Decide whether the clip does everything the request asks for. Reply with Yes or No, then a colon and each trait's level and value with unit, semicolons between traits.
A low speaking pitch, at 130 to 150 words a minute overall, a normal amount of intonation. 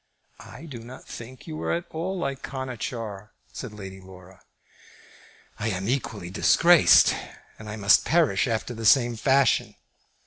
Yes: low, 115 Hz; average, 145 wpm; average, 5.0 semitones